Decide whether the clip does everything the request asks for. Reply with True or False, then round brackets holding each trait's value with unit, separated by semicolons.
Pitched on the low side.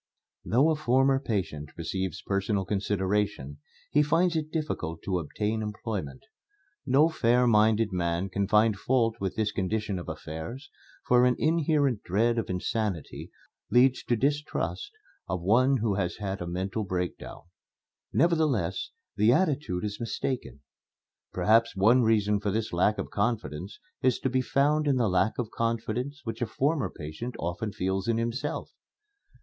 True (110 Hz)